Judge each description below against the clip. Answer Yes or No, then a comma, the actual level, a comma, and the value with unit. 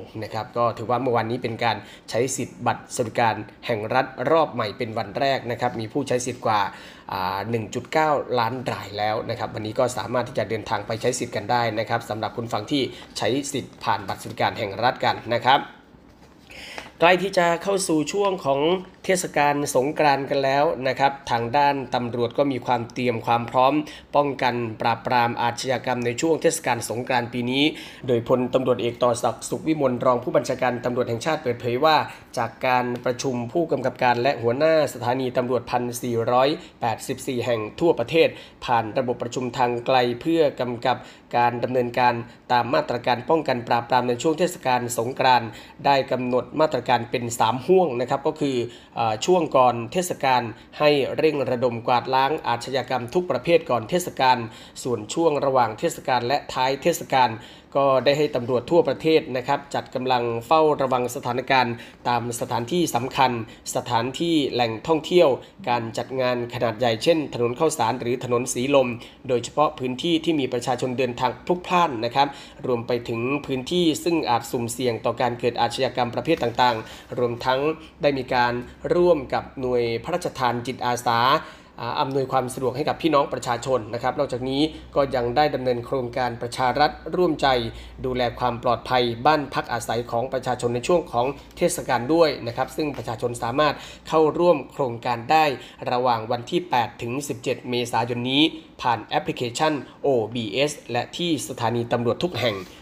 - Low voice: Yes, low, 125 Hz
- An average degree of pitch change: Yes, average, 3.3 semitones